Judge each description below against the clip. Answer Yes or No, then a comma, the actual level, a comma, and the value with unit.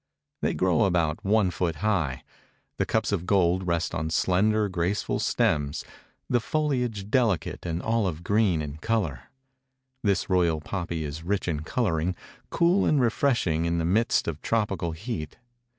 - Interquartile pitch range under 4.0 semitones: No, average, 4.8 semitones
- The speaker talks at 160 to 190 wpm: No, average, 150 wpm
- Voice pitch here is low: Yes, very low, 90 Hz